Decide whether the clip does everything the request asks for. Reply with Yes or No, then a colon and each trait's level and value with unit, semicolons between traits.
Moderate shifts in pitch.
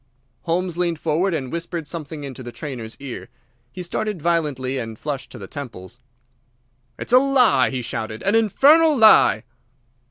No: wide, 6.4 semitones